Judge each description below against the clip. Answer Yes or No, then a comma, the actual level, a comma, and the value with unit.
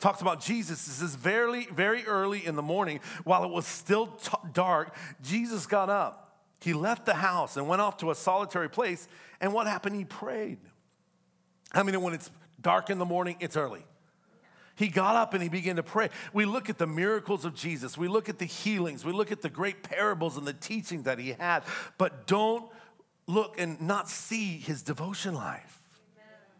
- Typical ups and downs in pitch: Yes, average, 3.6 semitones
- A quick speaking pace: No, average, 195 wpm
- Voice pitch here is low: No, medium, 185 Hz